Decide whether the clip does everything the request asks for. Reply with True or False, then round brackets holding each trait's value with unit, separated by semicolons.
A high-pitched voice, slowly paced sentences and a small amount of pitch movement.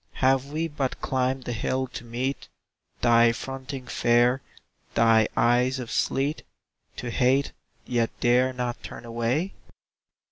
False (125 Hz; 130 wpm; 2.0 semitones)